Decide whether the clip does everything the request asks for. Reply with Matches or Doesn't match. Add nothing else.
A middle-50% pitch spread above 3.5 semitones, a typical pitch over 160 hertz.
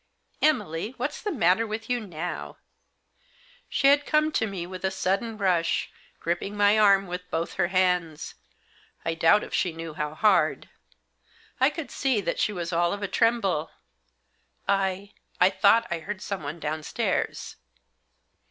Matches